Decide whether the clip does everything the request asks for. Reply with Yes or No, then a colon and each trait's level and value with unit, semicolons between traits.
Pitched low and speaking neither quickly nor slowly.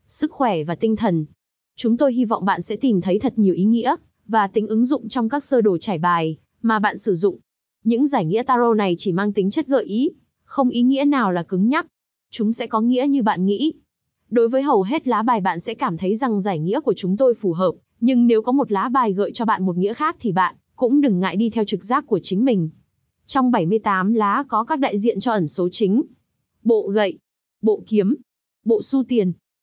No: high, 220 Hz; average, 235 wpm